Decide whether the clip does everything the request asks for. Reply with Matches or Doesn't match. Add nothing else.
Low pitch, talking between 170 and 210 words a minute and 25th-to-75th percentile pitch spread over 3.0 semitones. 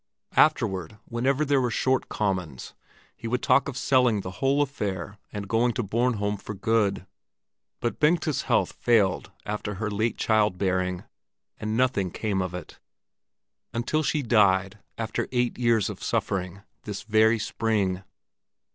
Doesn't match